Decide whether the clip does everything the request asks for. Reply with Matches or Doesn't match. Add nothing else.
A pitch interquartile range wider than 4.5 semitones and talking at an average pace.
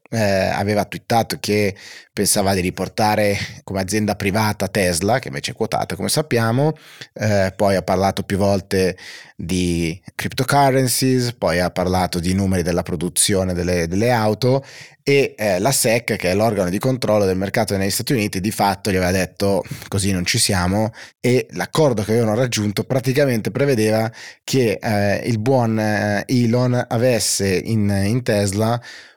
Doesn't match